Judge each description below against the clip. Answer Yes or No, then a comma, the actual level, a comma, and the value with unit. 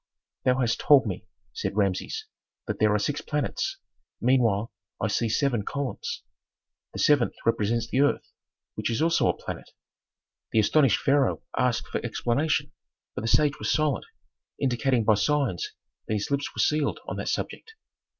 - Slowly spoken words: No, average, 160 wpm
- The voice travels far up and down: No, average, 4.4 semitones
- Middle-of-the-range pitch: No, low, 125 Hz